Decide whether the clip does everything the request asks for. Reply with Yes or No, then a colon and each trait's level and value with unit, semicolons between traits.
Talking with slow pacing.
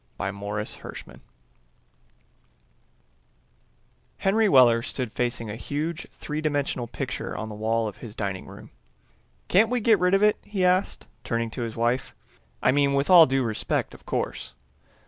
No: average, 155 wpm